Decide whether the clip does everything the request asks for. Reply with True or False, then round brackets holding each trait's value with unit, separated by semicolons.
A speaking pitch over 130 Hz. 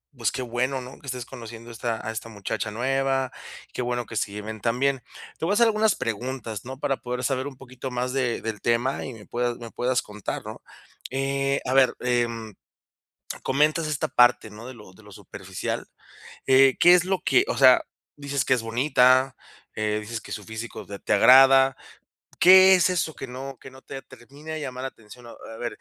False (125 Hz)